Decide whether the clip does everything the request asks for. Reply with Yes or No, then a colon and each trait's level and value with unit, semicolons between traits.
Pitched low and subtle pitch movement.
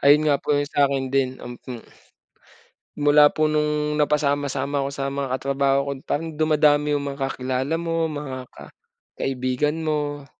No: medium, 145 Hz; narrow, 1.7 semitones